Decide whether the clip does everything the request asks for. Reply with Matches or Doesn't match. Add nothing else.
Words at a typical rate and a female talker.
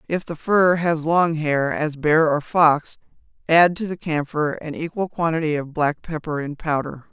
Matches